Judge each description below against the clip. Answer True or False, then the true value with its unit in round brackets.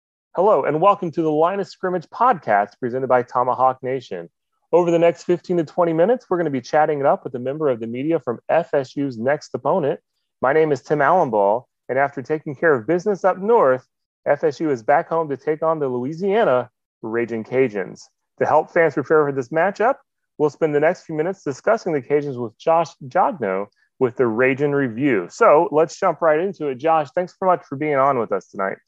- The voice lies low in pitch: False (155 Hz)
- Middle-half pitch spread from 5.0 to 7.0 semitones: False (4.4 semitones)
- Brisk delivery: True (210 wpm)